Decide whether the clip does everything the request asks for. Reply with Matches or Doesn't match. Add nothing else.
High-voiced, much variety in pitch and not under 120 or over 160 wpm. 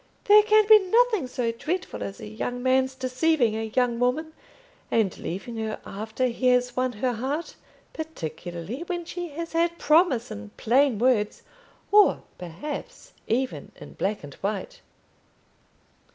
Matches